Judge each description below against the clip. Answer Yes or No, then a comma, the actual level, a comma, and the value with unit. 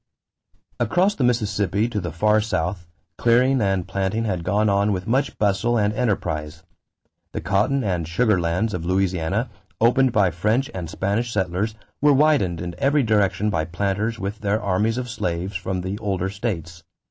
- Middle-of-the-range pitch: No, low, 100 Hz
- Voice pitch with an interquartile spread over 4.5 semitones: No, average, 4.0 semitones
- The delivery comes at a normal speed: Yes, average, 170 wpm